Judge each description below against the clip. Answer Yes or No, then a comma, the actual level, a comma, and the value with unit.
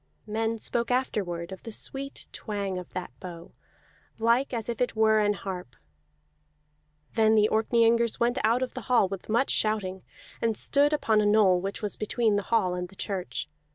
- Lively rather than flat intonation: No, average, 3.2 semitones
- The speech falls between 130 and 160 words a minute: No, average, 180 wpm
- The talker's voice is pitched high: Yes, high, 215 Hz